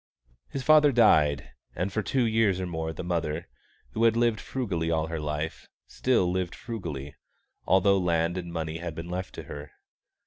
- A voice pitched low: Yes, very low, 90 Hz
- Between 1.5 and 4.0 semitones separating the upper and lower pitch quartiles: No, average, 5.2 semitones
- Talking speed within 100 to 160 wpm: No, average, 175 wpm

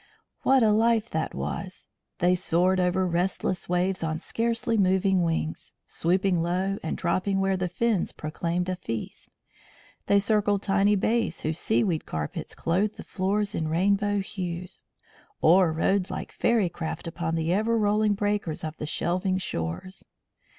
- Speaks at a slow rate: No, average, 155 wpm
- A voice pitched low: No, medium, 185 Hz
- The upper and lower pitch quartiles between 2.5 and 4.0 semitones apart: Yes, average, 3.1 semitones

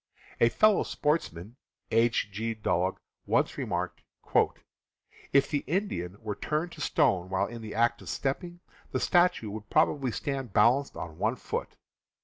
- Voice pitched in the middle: No, low, 120 Hz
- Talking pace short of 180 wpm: Yes, average, 145 wpm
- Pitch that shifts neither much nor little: No, wide, 6.1 semitones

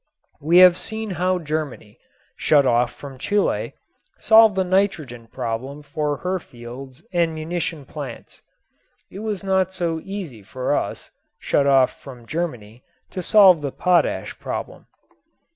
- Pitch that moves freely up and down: Yes, wide, 5.9 semitones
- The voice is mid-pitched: Yes, medium, 155 Hz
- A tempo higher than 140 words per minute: No, slow, 135 wpm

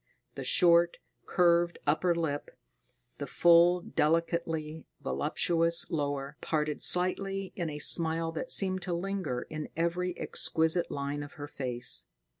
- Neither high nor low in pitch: Yes, medium, 165 Hz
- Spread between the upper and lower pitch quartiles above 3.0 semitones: No, average, 2.7 semitones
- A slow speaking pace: Yes, slow, 125 wpm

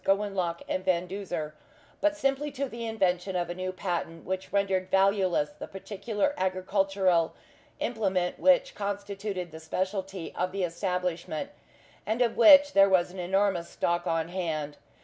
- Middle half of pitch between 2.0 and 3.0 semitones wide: Yes, narrow, 2.4 semitones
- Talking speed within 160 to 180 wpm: No, average, 150 wpm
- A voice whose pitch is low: No, high, 190 Hz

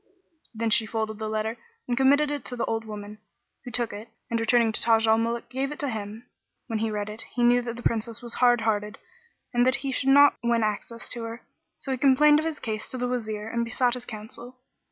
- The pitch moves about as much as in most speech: No, narrow, 2.3 semitones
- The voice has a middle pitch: No, high, 235 Hz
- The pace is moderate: No, fast, 235 wpm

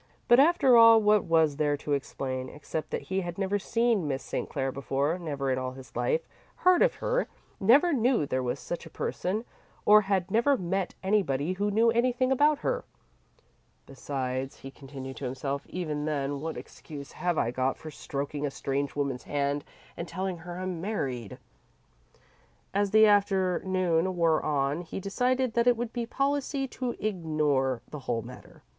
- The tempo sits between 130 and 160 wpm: No, average, 175 wpm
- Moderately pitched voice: Yes, medium, 175 Hz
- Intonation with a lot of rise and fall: Yes, wide, 7.7 semitones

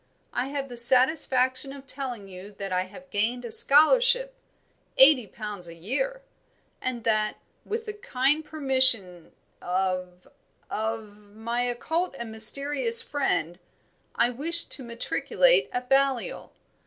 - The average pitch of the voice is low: No, very high, 250 Hz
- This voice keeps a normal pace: No, slow, 130 wpm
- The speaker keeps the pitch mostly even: No, average, 5.1 semitones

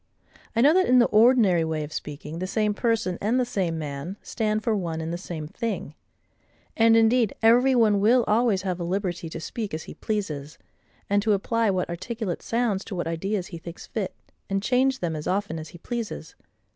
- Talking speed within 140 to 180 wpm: No, fast, 205 wpm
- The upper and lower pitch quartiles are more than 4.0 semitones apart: Yes, average, 5.1 semitones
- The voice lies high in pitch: Yes, high, 200 Hz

